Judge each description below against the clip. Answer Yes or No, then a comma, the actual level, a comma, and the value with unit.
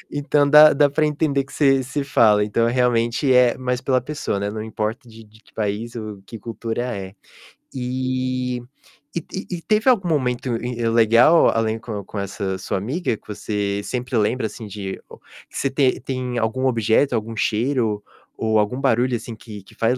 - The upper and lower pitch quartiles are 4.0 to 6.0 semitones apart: No, average, 3.4 semitones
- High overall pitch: No, low, 120 Hz